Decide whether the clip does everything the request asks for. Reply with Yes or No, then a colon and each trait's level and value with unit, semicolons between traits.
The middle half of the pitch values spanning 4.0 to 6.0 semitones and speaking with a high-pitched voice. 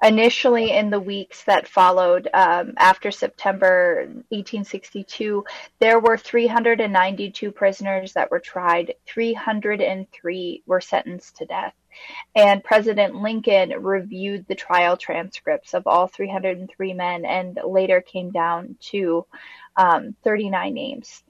No: average, 3.3 semitones; high, 200 Hz